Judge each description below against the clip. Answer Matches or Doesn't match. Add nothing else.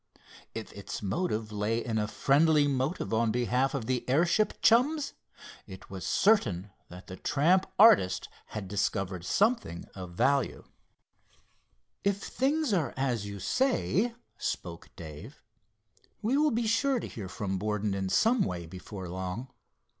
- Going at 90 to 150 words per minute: Matches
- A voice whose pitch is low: Matches